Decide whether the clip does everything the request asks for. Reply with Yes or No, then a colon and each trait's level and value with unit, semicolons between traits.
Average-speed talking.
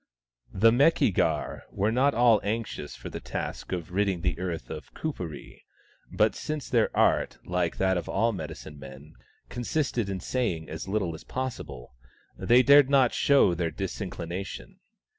Yes: average, 160 wpm